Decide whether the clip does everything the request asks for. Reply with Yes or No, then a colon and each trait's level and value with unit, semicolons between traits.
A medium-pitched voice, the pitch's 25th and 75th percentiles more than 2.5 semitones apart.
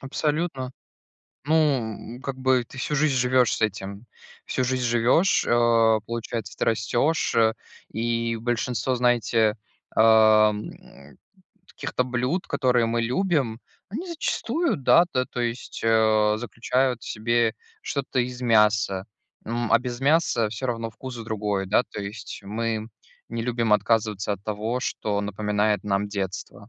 No: low, 115 Hz; average, 2.9 semitones